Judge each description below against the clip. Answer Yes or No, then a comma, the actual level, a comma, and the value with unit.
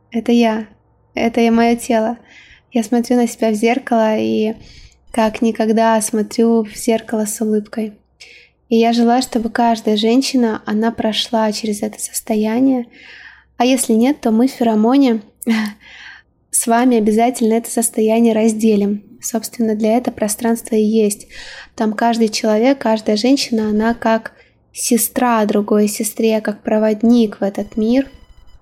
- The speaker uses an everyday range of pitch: No, narrow, 1.5 semitones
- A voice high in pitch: Yes, high, 225 Hz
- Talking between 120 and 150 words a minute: Yes, average, 135 wpm